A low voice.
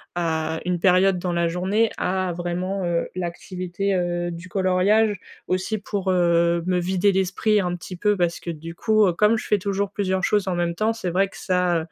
No: medium, 185 Hz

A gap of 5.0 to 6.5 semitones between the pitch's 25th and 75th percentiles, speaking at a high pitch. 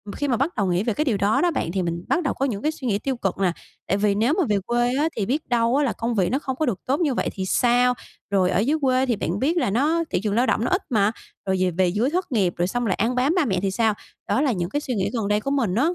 Yes: wide, 5.6 semitones; high, 235 Hz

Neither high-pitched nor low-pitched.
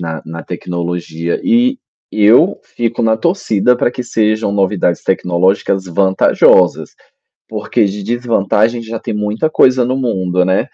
No: low, 105 Hz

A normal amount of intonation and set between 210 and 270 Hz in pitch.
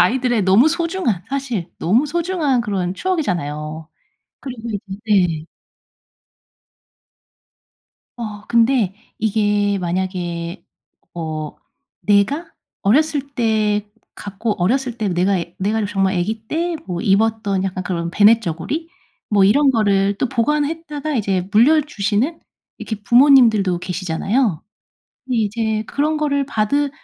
No: wide, 5.8 semitones; high, 215 Hz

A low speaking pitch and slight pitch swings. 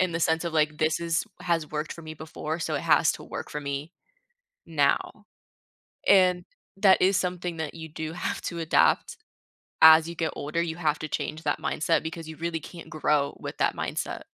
No: medium, 160 Hz; narrow, 1.6 semitones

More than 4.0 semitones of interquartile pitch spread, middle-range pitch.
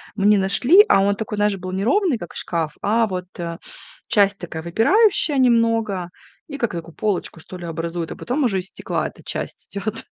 No: average, 4.7 semitones; high, 200 Hz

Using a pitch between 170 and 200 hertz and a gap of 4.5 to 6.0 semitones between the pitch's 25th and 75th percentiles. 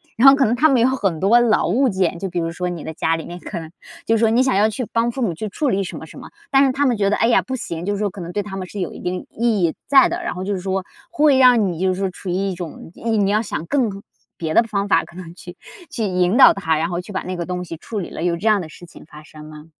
Yes: high, 195 Hz; average, 4.9 semitones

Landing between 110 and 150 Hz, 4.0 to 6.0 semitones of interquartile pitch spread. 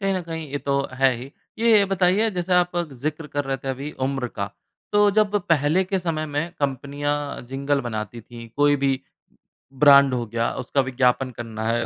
Yes: medium, 140 Hz; average, 4.7 semitones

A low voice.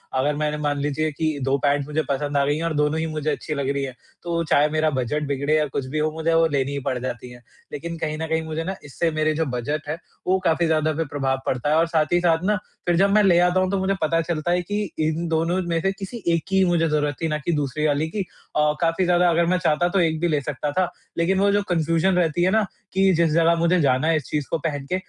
No: medium, 160 Hz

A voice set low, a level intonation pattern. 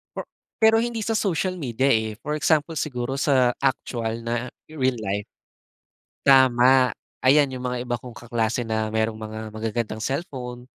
No: low, 125 Hz; average, 3.3 semitones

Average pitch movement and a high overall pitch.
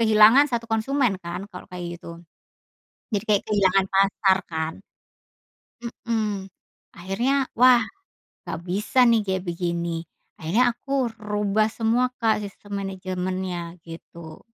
Yes: average, 3.8 semitones; high, 200 Hz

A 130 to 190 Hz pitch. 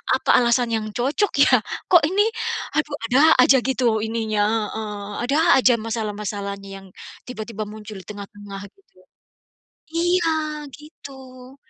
No: high, 230 Hz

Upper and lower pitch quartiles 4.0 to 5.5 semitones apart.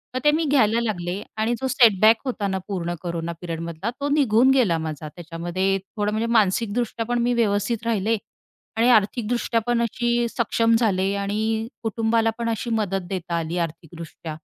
Yes: average, 4.6 semitones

